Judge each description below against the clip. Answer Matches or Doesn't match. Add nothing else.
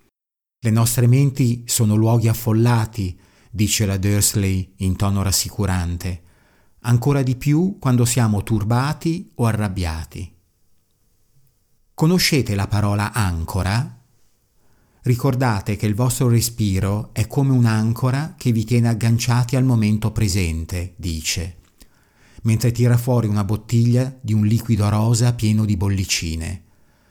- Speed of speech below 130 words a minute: Matches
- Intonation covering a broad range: Doesn't match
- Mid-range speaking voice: Doesn't match